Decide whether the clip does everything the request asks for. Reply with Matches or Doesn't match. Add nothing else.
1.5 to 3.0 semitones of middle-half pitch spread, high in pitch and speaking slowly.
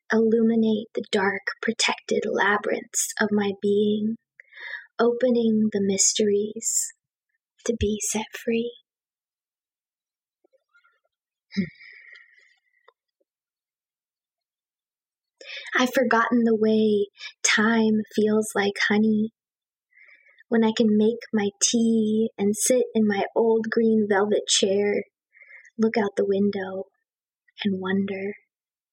Matches